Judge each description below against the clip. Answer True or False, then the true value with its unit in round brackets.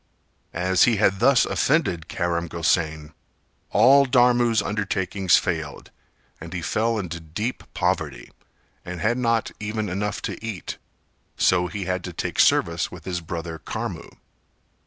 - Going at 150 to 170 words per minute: False (135 wpm)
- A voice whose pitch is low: True (95 Hz)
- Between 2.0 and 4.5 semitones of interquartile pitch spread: False (4.9 semitones)